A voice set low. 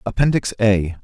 Yes: low, 110 Hz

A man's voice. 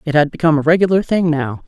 No: female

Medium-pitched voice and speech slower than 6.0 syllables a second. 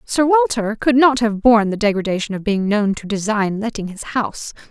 No: high, 220 Hz; 5.4 syllables/s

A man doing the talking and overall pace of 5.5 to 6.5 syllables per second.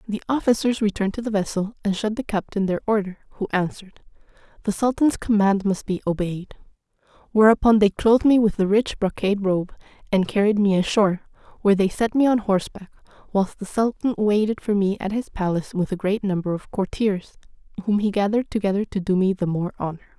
No: female; 6.0 syllables/s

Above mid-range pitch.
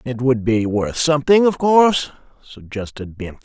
No: low, 130 Hz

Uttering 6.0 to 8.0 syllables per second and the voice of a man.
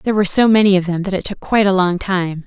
No: 7.0 syllables/s; female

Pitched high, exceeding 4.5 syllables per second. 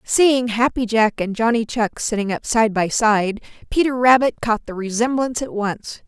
Yes: high, 225 Hz; 4.7 syllables/s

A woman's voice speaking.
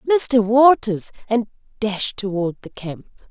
Yes: female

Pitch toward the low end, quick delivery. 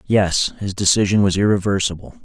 No: low, 100 Hz; slow, 135 wpm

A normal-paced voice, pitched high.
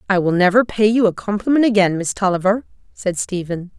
Yes: average, 190 wpm; high, 200 Hz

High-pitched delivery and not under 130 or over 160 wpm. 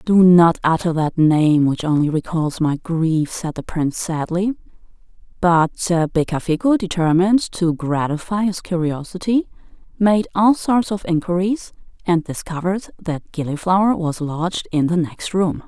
No: medium, 175 Hz; average, 140 wpm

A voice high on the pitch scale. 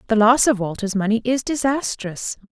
Yes: high, 225 Hz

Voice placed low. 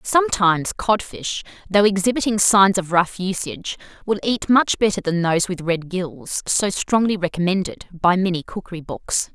No: high, 190 Hz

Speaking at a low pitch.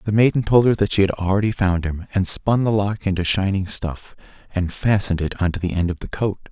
Yes: very low, 95 Hz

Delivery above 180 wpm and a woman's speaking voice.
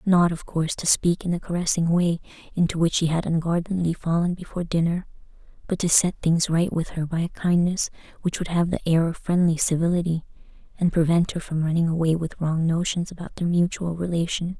Yes: average, 195 wpm; female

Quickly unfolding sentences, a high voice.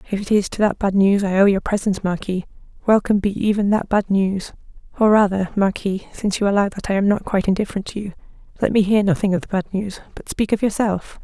Yes: fast, 235 wpm; high, 200 Hz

